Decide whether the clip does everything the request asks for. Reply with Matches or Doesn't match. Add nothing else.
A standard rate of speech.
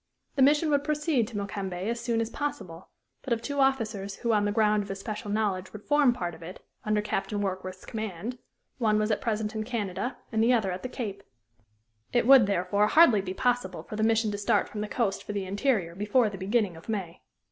Doesn't match